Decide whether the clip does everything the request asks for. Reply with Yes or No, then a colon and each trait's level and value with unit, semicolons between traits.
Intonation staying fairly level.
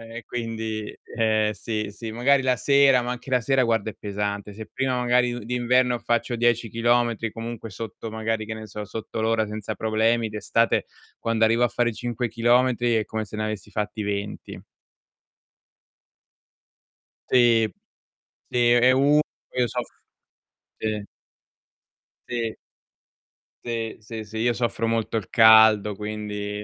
Yes: narrow, 1.9 semitones